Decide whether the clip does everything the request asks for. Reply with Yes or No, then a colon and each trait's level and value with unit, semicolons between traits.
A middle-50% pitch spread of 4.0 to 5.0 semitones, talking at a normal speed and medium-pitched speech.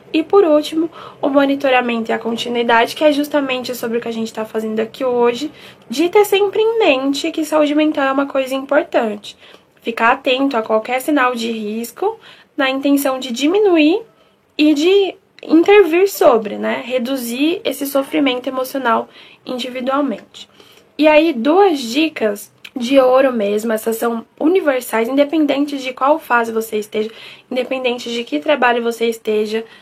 No: average, 4.5 semitones; average, 150 wpm; very high, 270 Hz